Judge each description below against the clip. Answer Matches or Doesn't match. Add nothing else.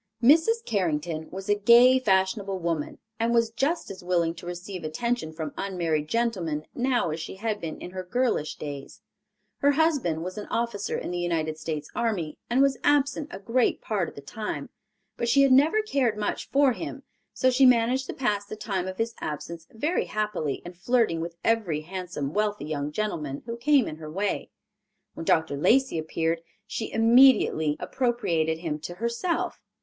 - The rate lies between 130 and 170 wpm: Doesn't match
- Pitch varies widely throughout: Matches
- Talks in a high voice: Matches